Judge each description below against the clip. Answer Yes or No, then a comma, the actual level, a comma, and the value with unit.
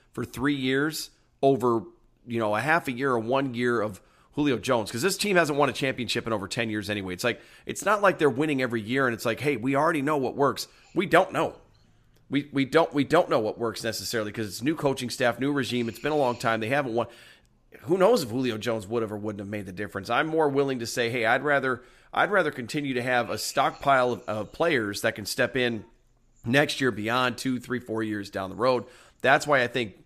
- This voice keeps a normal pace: No, fast, 245 wpm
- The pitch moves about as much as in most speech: Yes, average, 3.5 semitones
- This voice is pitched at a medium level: No, low, 125 Hz